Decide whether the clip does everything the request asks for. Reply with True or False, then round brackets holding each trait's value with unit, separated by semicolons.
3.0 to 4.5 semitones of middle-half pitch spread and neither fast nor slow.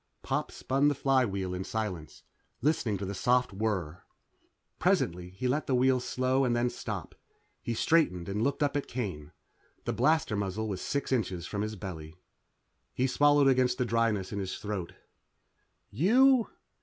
False (5.6 semitones; 160 wpm)